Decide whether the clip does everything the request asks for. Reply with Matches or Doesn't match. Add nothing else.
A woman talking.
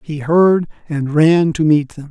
Doesn't match